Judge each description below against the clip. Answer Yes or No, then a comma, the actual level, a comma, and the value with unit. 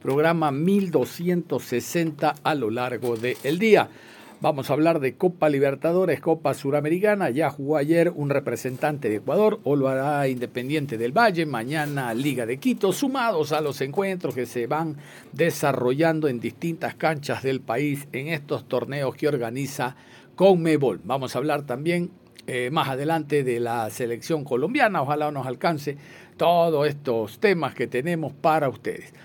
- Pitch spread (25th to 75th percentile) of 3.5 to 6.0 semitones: Yes, average, 4.2 semitones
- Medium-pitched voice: Yes, medium, 145 Hz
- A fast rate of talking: No, average, 150 wpm